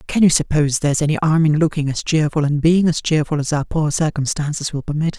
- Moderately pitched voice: Yes, medium, 150 Hz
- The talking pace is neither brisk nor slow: No, fast, 230 wpm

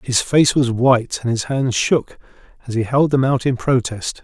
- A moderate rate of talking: No, fast, 210 wpm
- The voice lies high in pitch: No, low, 125 Hz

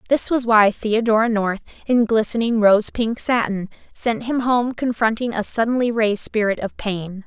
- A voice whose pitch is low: No, high, 225 Hz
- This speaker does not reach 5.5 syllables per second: Yes, 4.7 syllables/s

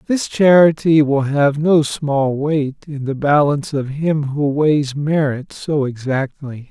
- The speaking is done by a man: Yes, male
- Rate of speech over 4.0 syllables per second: No, 3.7 syllables/s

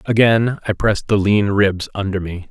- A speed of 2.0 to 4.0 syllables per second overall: No, 4.9 syllables/s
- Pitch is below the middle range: Yes, low, 100 Hz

